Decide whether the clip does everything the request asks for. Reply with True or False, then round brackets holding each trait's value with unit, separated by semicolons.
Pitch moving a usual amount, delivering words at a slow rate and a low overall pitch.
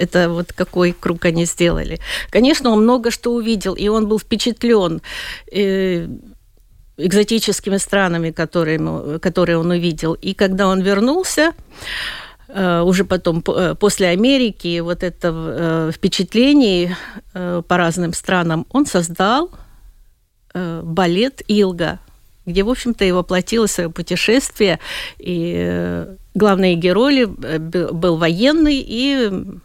False (3.9 semitones; 105 wpm; 185 Hz)